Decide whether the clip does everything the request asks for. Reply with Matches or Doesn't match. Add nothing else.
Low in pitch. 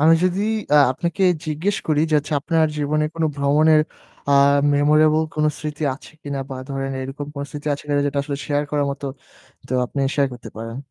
Doesn't match